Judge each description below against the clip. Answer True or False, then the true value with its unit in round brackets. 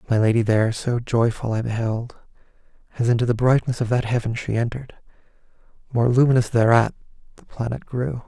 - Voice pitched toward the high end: False (120 Hz)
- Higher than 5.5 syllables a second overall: True (5.8 syllables/s)